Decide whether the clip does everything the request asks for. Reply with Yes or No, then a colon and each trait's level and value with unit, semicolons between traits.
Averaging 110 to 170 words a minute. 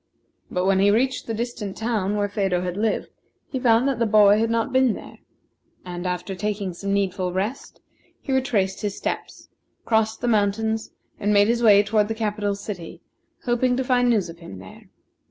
No: average, 190 wpm